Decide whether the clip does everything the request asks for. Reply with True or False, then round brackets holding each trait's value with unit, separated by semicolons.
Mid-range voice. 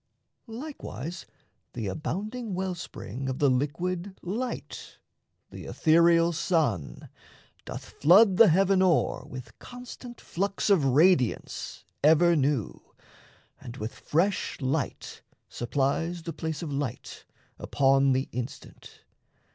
True (165 Hz)